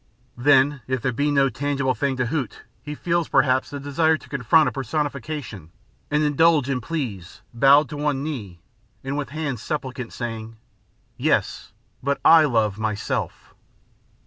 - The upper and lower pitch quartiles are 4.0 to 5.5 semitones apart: No, average, 3.5 semitones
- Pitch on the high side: No, low, 135 Hz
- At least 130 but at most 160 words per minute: Yes, average, 150 wpm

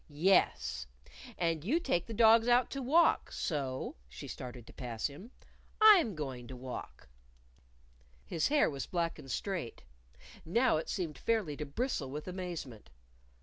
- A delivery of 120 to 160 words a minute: Yes, average, 145 wpm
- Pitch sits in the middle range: Yes, medium, 165 Hz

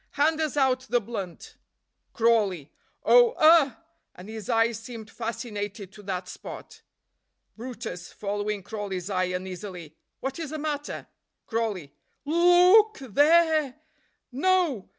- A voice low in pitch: No, high, 230 Hz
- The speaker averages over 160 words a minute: No, average, 140 wpm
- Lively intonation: Yes, wide, 6.8 semitones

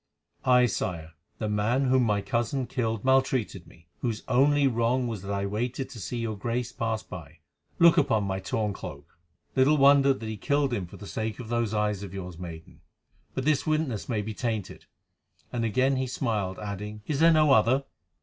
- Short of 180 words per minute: No, average, 190 wpm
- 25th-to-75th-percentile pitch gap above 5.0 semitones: No, average, 4.2 semitones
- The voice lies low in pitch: Yes, low, 115 Hz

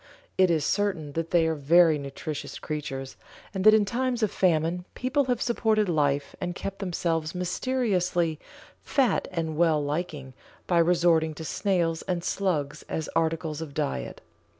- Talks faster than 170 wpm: No, average, 150 wpm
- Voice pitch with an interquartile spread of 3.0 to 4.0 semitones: Yes, average, 3.5 semitones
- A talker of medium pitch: Yes, medium, 170 Hz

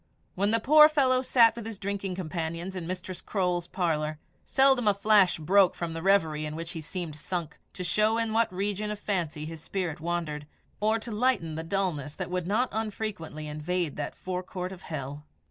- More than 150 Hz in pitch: Yes, medium, 185 Hz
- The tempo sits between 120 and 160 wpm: No, average, 190 wpm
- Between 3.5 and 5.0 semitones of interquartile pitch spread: Yes, average, 4.6 semitones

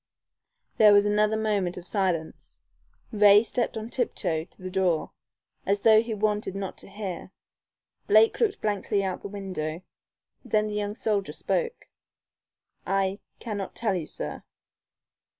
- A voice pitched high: Yes, high, 205 Hz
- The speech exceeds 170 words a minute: No, average, 145 wpm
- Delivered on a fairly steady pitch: Yes, narrow, 2.2 semitones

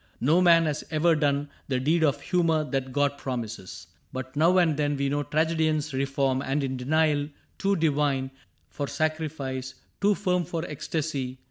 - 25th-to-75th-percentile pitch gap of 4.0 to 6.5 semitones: No, average, 3.0 semitones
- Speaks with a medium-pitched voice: Yes, medium, 145 Hz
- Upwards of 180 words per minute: No, average, 160 wpm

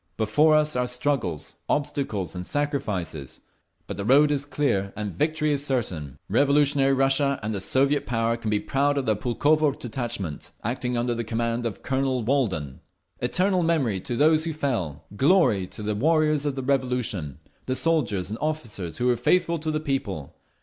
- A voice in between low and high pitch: No, low, 125 Hz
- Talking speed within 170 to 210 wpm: Yes, average, 175 wpm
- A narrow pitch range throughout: No, wide, 5.4 semitones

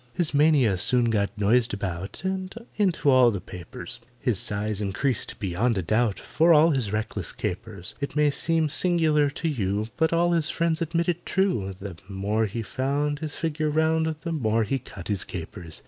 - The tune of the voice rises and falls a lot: Yes, wide, 7.7 semitones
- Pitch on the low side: Yes, low, 130 Hz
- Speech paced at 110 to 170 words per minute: No, average, 180 wpm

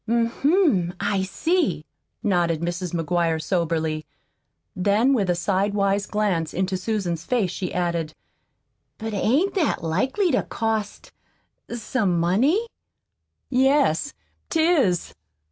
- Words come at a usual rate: No, slow, 110 wpm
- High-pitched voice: Yes, high, 200 Hz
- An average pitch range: No, wide, 6.3 semitones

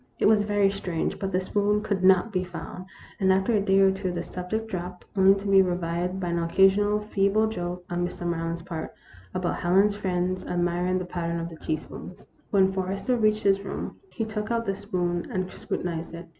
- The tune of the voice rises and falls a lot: No, narrow, 2.4 semitones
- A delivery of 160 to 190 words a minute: No, average, 200 wpm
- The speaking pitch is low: No, high, 190 Hz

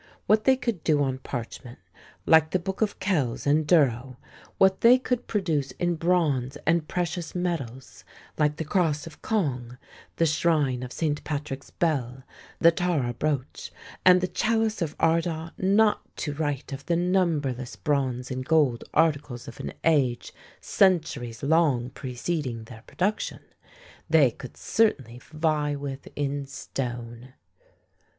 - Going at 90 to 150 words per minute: Yes, average, 140 wpm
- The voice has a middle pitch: Yes, medium, 150 Hz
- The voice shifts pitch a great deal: No, average, 4.8 semitones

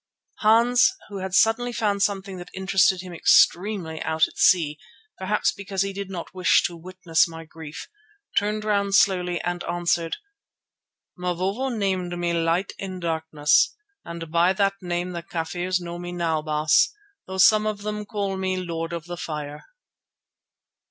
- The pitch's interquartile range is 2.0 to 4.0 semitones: Yes, average, 2.8 semitones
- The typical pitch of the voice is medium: Yes, medium, 180 Hz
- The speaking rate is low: No, average, 155 wpm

